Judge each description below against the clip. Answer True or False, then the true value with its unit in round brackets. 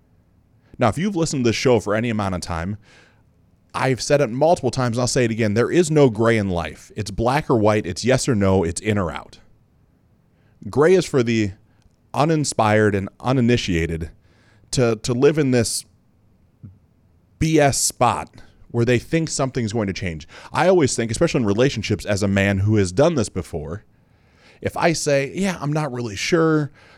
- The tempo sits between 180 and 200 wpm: True (185 wpm)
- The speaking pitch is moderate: False (115 Hz)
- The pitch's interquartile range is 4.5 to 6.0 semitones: True (5.0 semitones)